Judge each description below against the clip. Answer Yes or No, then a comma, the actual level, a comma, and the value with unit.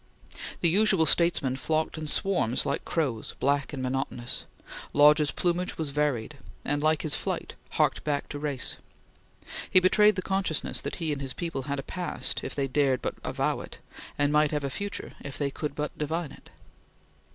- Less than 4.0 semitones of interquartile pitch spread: Yes, average, 3.1 semitones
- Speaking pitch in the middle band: Yes, medium, 150 Hz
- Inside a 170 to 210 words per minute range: Yes, average, 180 wpm